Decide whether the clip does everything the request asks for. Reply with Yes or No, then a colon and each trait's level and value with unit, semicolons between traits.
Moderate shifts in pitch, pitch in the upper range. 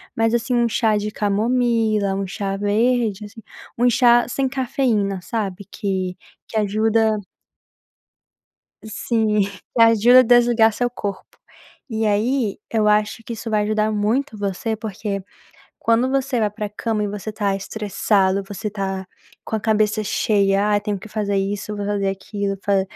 No: narrow, 2.1 semitones; high, 215 Hz